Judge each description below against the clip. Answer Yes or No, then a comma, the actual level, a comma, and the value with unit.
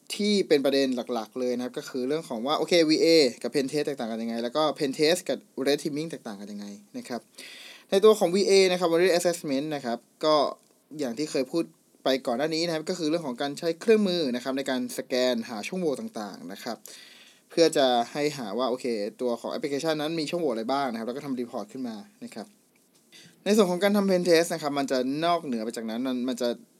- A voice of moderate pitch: Yes, medium, 150 Hz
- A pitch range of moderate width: No, wide, 5.8 semitones